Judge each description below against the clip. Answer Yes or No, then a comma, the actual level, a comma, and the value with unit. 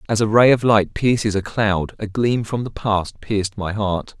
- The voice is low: Yes, low, 105 Hz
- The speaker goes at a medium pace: No, fast, 230 wpm